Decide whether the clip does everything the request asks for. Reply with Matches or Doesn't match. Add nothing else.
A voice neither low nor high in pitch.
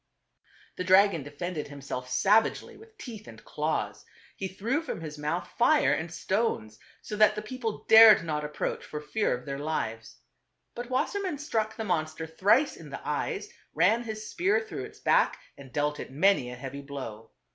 Matches